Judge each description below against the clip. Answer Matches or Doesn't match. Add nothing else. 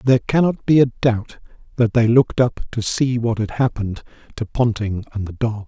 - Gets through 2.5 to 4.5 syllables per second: Doesn't match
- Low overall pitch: Matches